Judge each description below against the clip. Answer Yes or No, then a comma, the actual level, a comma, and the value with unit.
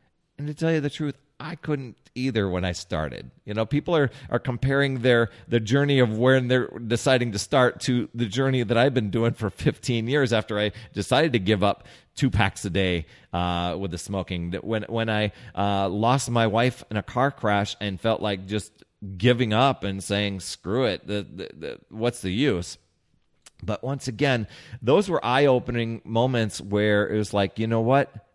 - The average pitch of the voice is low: Yes, low, 115 Hz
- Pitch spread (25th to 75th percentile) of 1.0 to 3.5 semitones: No, average, 4.1 semitones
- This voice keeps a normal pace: Yes, average, 195 wpm